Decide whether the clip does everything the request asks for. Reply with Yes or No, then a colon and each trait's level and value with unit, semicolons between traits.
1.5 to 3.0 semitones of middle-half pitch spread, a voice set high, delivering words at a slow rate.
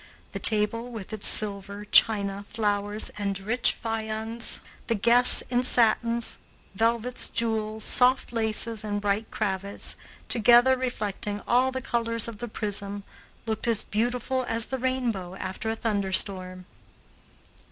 Yes: narrow, 2.5 semitones; high, 220 Hz; slow, 130 wpm